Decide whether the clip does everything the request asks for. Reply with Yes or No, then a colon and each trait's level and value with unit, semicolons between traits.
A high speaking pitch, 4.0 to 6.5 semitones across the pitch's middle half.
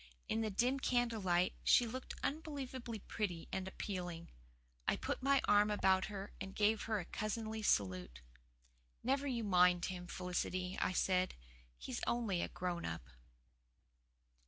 Yes: high, 200 Hz; average, 4.4 semitones